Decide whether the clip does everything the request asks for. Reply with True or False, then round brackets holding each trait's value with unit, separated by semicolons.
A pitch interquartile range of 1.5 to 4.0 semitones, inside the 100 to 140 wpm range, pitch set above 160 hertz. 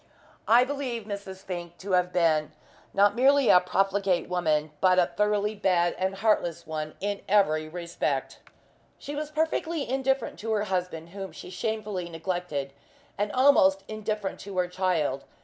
False (3.6 semitones; 150 wpm; 190 Hz)